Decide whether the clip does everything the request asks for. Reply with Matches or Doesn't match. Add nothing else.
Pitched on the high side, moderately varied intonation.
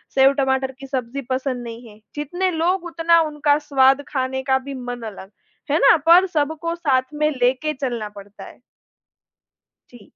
Matches